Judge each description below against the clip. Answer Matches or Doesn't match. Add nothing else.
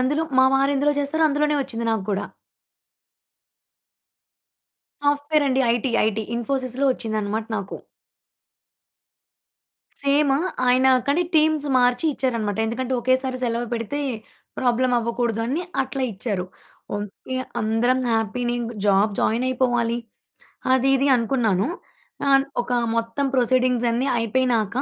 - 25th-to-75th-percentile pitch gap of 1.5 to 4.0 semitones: Matches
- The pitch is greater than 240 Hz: Matches